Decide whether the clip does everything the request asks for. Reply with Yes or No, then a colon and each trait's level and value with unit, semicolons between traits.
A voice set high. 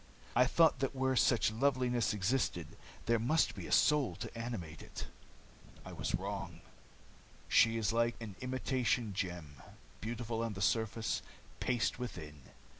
No: low, 115 Hz